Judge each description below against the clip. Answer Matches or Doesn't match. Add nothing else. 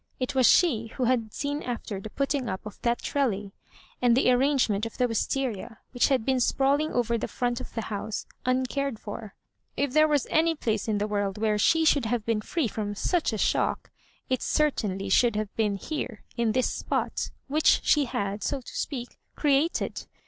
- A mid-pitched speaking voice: Doesn't match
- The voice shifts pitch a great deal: Doesn't match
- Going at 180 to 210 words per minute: Matches